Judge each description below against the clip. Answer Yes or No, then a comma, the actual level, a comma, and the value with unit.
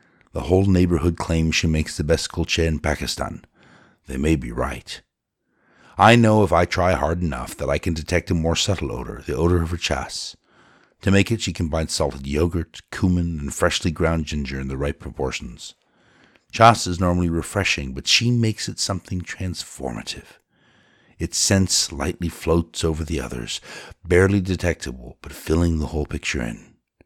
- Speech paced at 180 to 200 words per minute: No, average, 170 wpm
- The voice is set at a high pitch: No, very low, 85 Hz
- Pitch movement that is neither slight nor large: Yes, average, 3.3 semitones